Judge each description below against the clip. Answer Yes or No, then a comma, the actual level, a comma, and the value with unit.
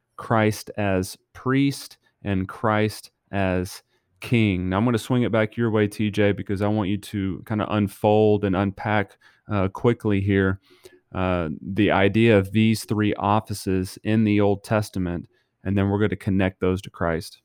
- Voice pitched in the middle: No, low, 105 Hz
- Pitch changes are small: Yes, narrow, 2.1 semitones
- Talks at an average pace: Yes, average, 170 wpm